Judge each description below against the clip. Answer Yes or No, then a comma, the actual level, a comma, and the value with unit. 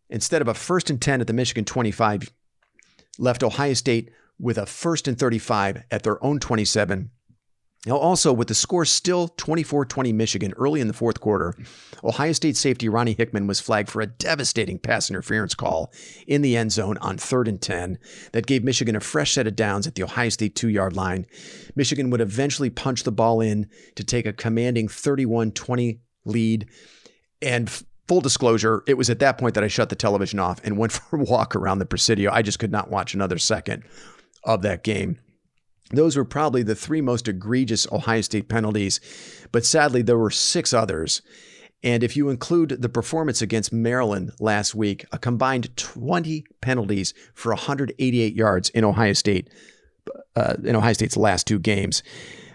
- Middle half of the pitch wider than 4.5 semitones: No, average, 3.6 semitones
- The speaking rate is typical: Yes, average, 185 wpm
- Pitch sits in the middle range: No, low, 115 Hz